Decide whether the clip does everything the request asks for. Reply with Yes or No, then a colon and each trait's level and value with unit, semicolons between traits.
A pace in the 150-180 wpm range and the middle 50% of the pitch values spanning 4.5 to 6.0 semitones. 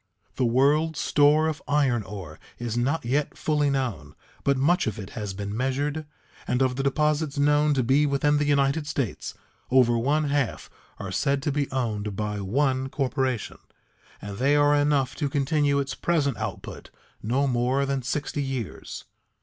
No: average, 165 wpm; average, 3.3 semitones